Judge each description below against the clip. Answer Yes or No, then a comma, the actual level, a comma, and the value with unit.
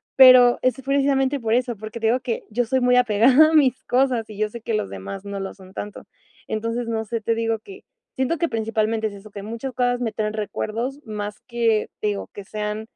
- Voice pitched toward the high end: Yes, high, 230 Hz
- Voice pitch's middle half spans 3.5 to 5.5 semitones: No, average, 2.8 semitones